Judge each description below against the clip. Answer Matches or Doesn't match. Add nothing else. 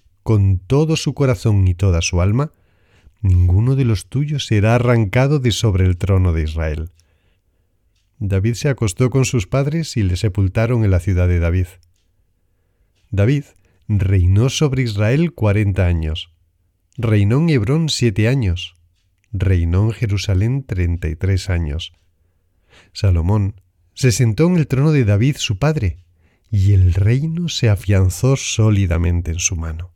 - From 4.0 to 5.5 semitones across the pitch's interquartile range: Matches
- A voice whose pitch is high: Doesn't match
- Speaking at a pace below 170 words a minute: Matches